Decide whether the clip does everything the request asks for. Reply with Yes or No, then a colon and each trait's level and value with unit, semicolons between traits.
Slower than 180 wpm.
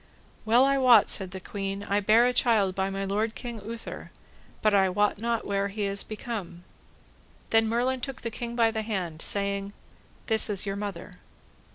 No: average, 185 wpm